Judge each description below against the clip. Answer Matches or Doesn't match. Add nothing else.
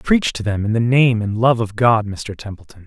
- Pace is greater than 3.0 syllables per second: Matches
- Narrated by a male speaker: Matches